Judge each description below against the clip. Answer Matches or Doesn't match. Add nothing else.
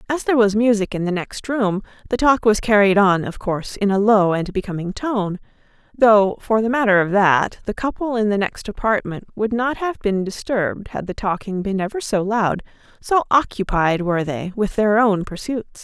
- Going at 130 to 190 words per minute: Doesn't match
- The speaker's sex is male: Doesn't match